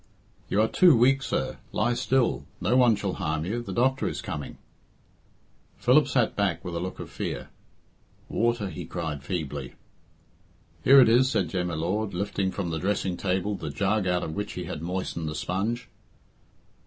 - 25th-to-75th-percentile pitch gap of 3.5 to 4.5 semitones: No, average, 5.2 semitones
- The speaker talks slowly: No, average, 180 wpm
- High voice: No, very low, 95 Hz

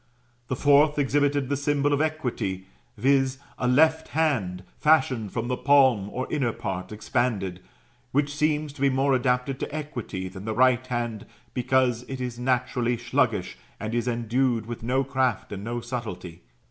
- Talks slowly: No, average, 160 wpm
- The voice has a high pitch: No, low, 125 Hz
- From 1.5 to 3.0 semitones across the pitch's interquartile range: No, average, 3.4 semitones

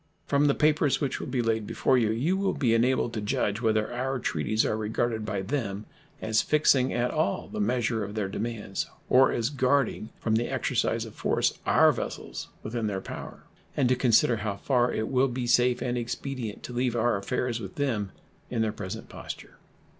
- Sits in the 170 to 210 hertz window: No, low, 120 Hz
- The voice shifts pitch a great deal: No, average, 2.9 semitones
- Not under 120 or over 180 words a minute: No, average, 195 wpm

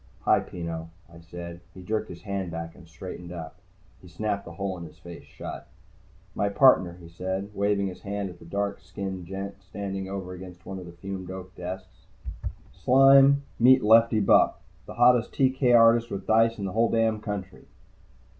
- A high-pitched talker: No, very low, 95 Hz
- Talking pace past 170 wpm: Yes, average, 185 wpm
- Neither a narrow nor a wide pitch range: Yes, average, 3.4 semitones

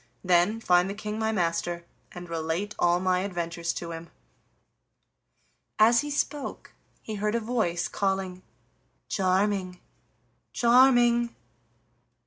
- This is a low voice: No, high, 190 Hz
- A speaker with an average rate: No, slow, 115 wpm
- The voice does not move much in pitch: No, average, 4.1 semitones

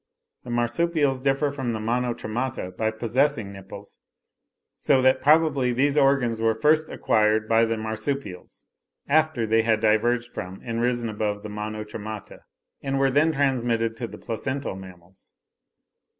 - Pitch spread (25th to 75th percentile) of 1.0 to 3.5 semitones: No, average, 4.0 semitones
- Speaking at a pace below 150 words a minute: Yes, average, 140 wpm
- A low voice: Yes, low, 115 Hz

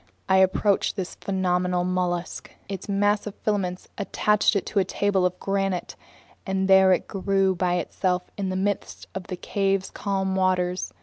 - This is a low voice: No, high, 190 Hz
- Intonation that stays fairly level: Yes, narrow, 1.4 semitones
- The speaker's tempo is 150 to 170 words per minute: Yes, average, 165 wpm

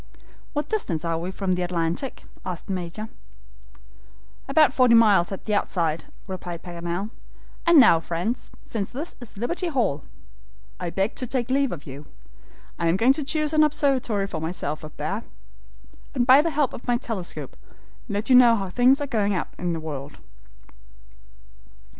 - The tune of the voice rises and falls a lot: Yes, wide, 7.0 semitones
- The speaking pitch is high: Yes, high, 205 Hz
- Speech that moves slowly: No, average, 170 wpm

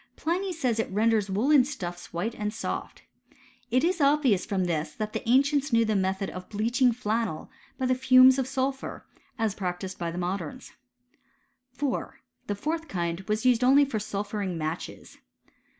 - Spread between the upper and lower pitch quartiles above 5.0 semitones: Yes, wide, 5.4 semitones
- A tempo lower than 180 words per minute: Yes, average, 165 wpm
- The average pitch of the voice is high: Yes, high, 225 Hz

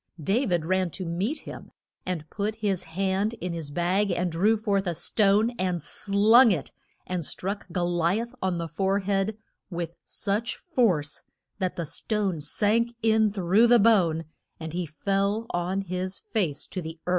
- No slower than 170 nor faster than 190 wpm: Yes, average, 175 wpm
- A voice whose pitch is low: No, high, 190 Hz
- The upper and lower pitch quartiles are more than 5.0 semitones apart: No, average, 3.5 semitones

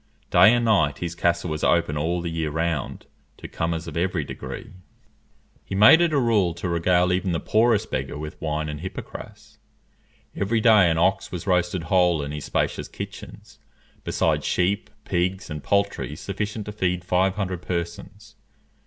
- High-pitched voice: No, very low, 90 Hz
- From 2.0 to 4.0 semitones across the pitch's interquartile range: Yes, average, 3.4 semitones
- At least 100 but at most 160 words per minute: No, average, 170 wpm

